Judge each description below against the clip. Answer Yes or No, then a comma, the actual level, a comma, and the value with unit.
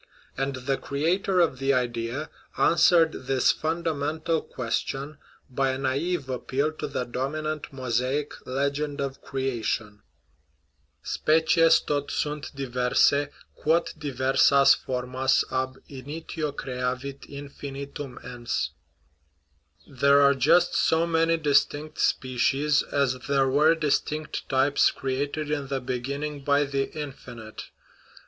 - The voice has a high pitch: No, medium, 140 Hz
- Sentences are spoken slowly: Yes, slow, 125 wpm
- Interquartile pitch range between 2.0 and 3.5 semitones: Yes, narrow, 2.6 semitones